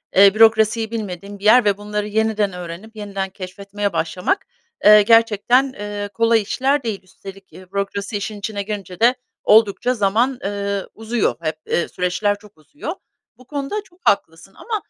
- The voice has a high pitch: Yes, high, 205 Hz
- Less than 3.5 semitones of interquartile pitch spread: Yes, narrow, 2.5 semitones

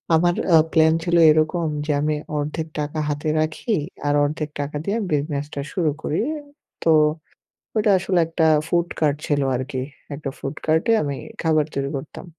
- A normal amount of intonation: No, narrow, 2.1 semitones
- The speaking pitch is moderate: Yes, medium, 155 Hz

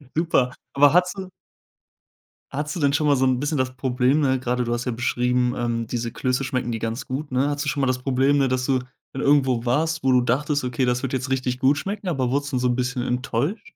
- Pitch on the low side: Yes, low, 130 Hz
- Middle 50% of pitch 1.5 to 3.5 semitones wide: Yes, narrow, 2.5 semitones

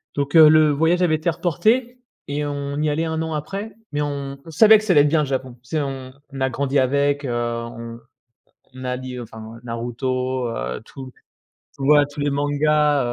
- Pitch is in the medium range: Yes, medium, 145 Hz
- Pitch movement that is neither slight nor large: Yes, average, 3.1 semitones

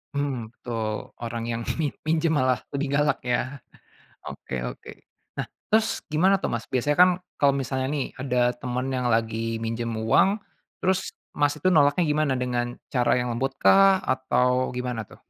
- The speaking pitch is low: Yes, low, 130 Hz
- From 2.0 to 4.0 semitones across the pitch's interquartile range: Yes, average, 3.4 semitones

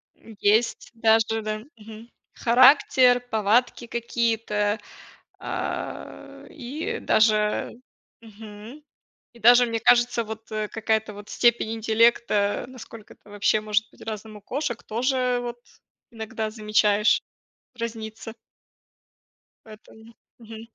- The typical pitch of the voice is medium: No, high, 225 Hz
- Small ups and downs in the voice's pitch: Yes, narrow, 1.8 semitones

